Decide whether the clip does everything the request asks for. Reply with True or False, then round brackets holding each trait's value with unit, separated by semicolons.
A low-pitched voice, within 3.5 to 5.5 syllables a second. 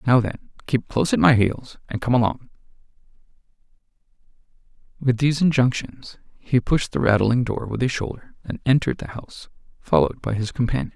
False (115 Hz; 5.7 syllables/s)